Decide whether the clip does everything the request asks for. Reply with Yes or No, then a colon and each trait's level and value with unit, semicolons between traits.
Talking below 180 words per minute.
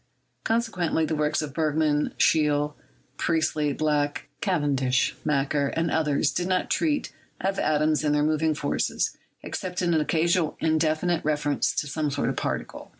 Yes: average, 150 wpm